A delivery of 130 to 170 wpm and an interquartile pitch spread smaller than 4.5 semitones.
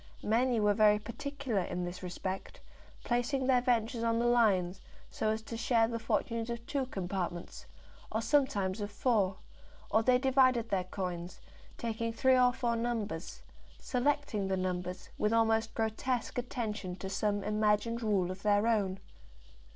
Yes: average, 150 wpm; average, 3.6 semitones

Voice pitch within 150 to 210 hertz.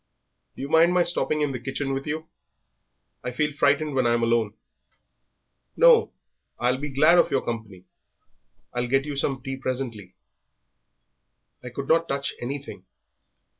No: low, 135 Hz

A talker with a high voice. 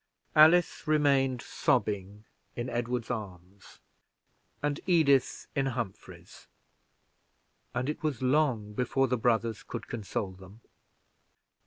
No: low, 120 Hz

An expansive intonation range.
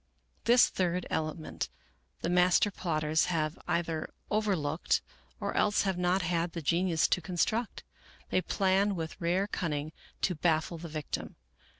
No: average, 2.8 semitones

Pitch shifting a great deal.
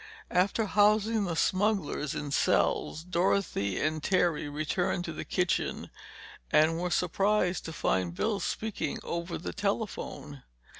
No: average, 4.4 semitones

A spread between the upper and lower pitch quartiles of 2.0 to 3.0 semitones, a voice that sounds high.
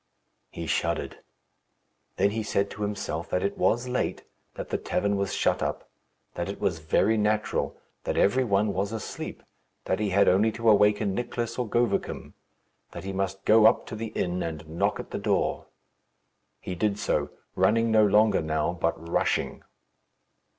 No: average, 2.7 semitones; low, 100 Hz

